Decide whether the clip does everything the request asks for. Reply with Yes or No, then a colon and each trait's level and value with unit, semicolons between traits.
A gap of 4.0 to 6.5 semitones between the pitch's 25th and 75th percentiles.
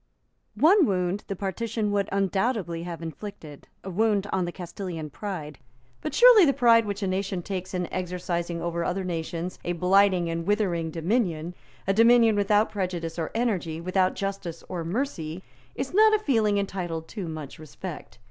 No: average, 3.6 semitones